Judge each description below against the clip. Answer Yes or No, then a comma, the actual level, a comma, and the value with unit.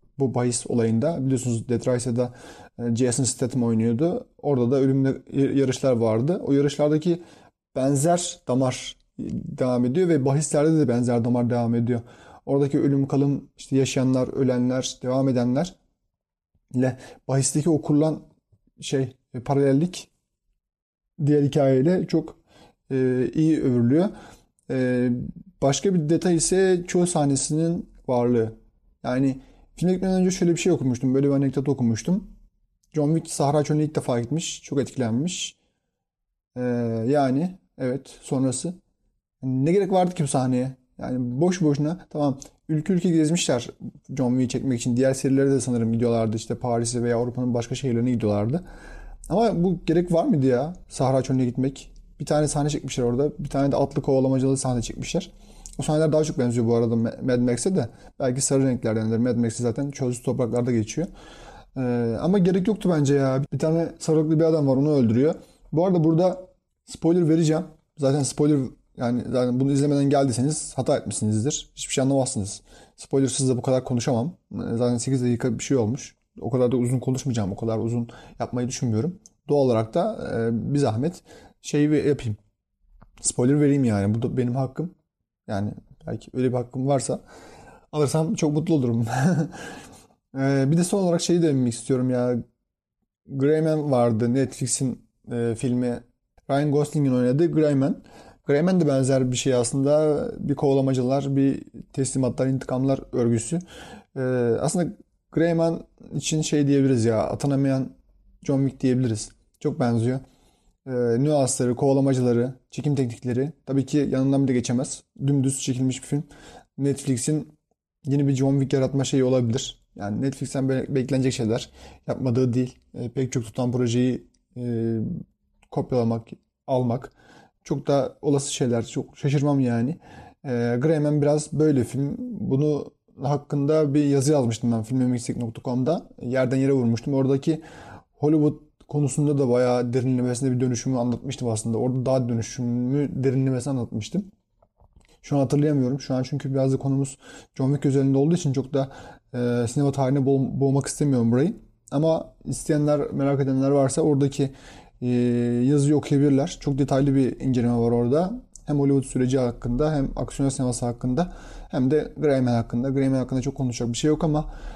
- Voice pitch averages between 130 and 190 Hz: Yes, low, 135 Hz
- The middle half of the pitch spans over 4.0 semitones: No, average, 3.1 semitones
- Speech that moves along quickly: Yes, fast, 145 wpm